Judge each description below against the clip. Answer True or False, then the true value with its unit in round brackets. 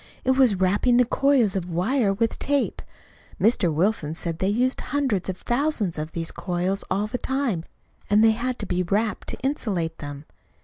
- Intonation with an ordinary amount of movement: False (5.8 semitones)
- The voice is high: True (205 Hz)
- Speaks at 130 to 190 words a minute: True (180 wpm)